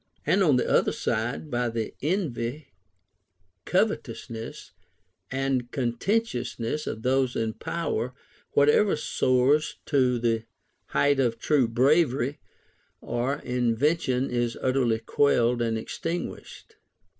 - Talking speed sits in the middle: No, slow, 105 wpm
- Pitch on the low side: Yes, low, 125 Hz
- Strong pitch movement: No, average, 3.6 semitones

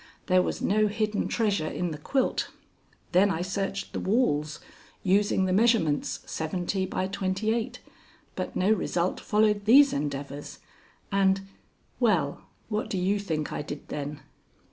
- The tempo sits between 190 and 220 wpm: No, average, 145 wpm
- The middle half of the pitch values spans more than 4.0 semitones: Yes, average, 4.9 semitones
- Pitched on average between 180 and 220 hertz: Yes, high, 190 Hz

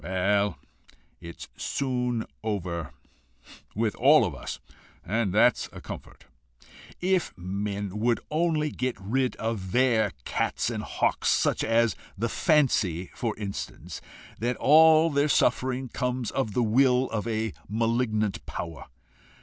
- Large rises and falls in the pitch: No, average, 4.1 semitones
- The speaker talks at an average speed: No, slow, 125 wpm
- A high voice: No, low, 115 Hz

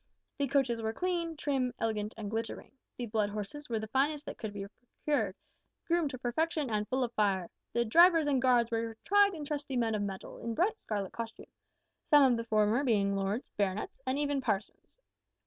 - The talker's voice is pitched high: Yes, high, 235 Hz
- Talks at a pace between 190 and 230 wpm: Yes, average, 195 wpm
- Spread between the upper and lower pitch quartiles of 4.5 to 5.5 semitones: Yes, average, 5.2 semitones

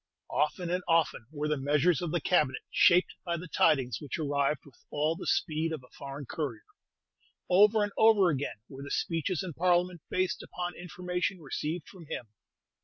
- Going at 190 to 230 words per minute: No, average, 180 wpm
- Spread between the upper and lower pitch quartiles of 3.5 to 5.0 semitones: Yes, average, 3.8 semitones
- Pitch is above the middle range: No, medium, 165 Hz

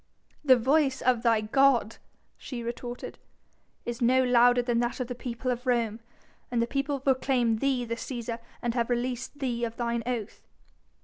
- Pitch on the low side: No, high, 245 Hz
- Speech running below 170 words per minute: No, average, 175 wpm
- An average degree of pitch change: No, narrow, 1.6 semitones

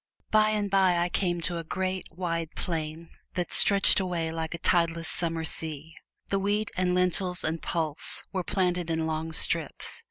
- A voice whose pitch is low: No, medium, 170 Hz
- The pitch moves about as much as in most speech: No, narrow, 2.3 semitones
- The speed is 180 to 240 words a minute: No, average, 170 wpm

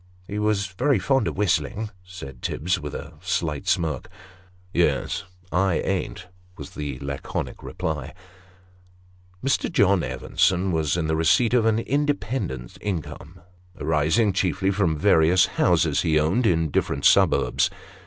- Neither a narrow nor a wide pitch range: Yes, average, 4.5 semitones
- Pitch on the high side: No, very low, 90 Hz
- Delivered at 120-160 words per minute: Yes, average, 140 wpm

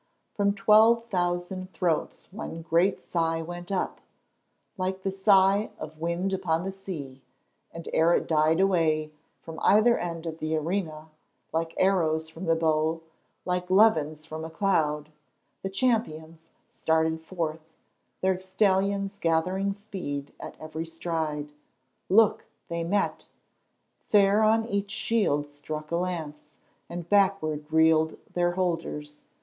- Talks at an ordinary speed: No, slow, 130 wpm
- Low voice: No, medium, 170 Hz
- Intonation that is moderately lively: Yes, average, 3.4 semitones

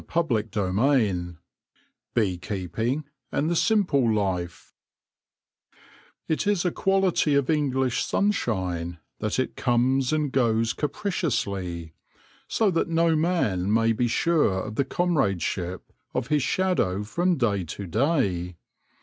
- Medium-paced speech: No, slow, 120 wpm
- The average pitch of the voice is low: Yes, low, 120 Hz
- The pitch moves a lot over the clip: Yes, wide, 8.4 semitones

